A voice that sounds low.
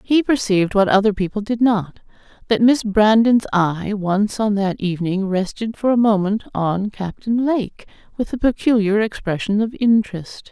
No: high, 210 Hz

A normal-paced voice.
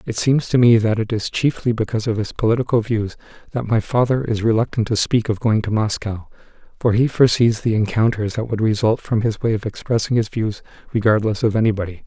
No: fast, 210 wpm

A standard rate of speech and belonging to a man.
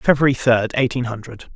Yes: average, 155 wpm; male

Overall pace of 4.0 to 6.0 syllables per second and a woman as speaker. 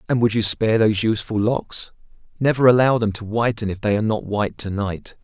No: 5.9 syllables/s; male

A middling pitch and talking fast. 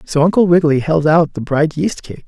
Yes: medium, 155 Hz; fast, 240 wpm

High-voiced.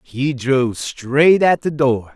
No: low, 135 Hz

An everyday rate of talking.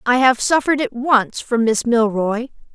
Yes: average, 175 wpm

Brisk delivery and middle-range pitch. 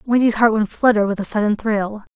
No: fast, 225 wpm; high, 215 Hz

